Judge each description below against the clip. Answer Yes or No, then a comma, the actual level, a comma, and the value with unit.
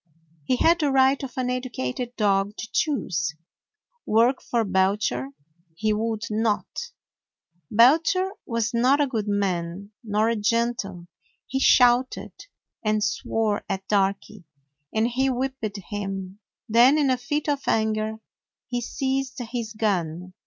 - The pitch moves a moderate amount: Yes, average, 3.9 semitones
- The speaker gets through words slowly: Yes, slow, 130 wpm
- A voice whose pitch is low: No, high, 225 Hz